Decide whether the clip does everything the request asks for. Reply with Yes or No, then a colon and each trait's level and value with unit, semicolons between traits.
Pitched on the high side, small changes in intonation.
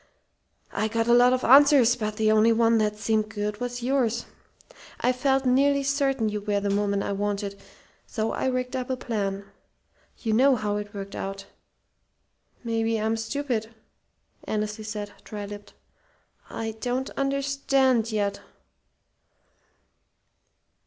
No: high, 225 Hz; average, 3.3 semitones